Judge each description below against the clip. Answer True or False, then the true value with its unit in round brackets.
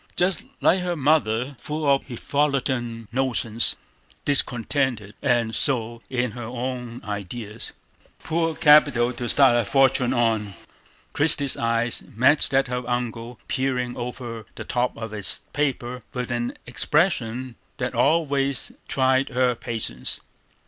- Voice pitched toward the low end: True (125 Hz)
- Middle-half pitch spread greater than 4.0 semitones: False (2.9 semitones)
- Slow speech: True (130 wpm)